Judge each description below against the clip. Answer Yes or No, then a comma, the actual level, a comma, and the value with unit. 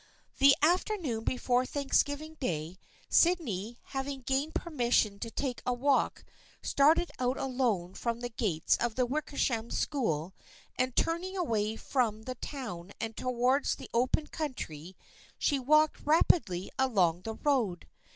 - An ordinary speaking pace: No, slow, 130 wpm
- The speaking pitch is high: Yes, very high, 250 Hz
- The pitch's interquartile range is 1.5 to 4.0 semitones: No, average, 4.5 semitones